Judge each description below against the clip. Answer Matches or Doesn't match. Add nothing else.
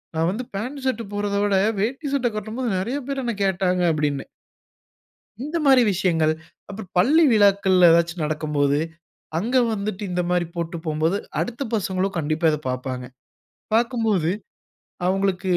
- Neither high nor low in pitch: Doesn't match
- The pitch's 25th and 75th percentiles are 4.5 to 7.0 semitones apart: Matches